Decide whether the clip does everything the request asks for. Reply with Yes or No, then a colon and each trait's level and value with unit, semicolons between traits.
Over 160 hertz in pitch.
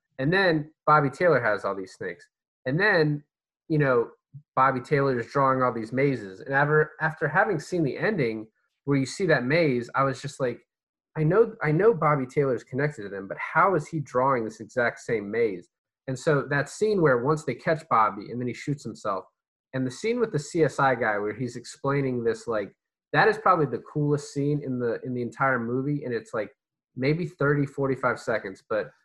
No: medium, 140 Hz